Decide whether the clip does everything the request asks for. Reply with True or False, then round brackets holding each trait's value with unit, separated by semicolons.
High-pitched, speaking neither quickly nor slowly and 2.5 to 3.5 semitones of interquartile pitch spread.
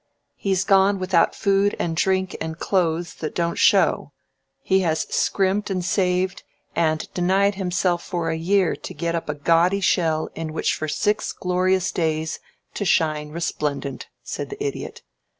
False (180 Hz; 155 wpm; 2.9 semitones)